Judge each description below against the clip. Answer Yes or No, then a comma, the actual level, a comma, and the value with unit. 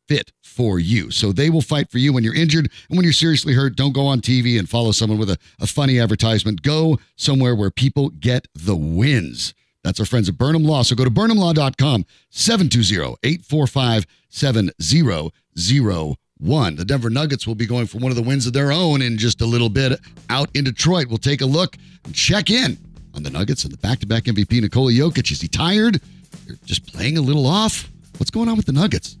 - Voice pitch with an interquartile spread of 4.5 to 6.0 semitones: Yes, average, 4.8 semitones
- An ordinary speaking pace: No, fast, 215 wpm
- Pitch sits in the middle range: No, low, 130 Hz